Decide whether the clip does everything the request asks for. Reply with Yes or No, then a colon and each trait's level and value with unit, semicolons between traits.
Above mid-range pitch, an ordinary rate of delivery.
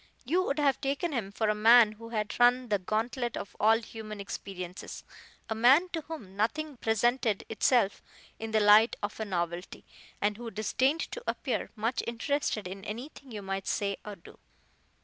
Yes: high, 225 Hz; average, 175 wpm